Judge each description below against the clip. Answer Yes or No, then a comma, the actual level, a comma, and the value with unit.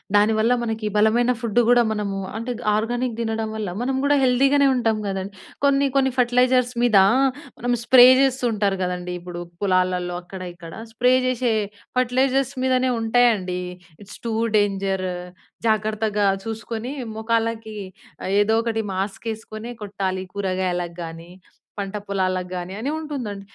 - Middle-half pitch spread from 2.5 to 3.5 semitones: No, average, 4.1 semitones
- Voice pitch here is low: No, high, 220 Hz